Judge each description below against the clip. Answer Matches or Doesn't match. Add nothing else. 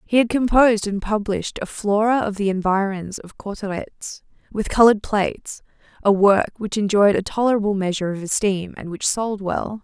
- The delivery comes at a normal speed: Matches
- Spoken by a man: Doesn't match